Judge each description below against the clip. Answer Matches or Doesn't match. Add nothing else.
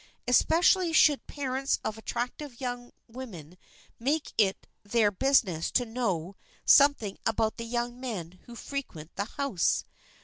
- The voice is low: Doesn't match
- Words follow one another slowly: Matches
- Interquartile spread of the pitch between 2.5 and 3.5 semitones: Doesn't match